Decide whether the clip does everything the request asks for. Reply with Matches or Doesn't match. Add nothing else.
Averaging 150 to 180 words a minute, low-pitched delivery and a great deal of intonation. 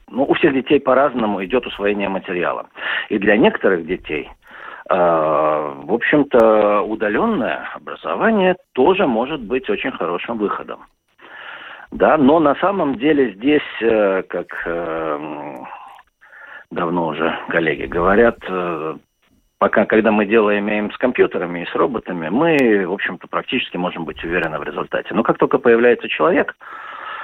Doesn't match